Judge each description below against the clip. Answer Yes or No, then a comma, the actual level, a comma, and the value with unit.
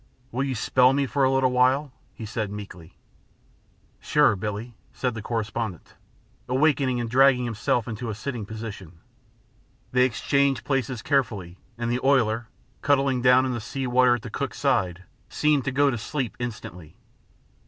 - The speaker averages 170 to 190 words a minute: No, average, 160 wpm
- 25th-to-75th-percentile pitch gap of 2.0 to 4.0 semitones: Yes, average, 3.4 semitones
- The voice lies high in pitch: No, low, 125 Hz